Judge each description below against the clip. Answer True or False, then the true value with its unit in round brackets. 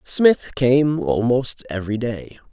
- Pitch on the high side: False (120 Hz)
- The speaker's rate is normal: False (120 wpm)